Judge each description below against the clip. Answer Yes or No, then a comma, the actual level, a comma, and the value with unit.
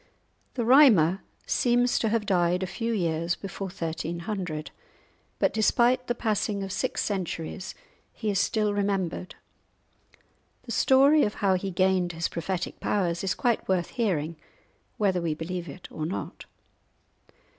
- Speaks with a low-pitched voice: No, high, 190 Hz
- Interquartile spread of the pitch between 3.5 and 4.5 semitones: Yes, average, 4.0 semitones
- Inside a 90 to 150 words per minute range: Yes, average, 140 wpm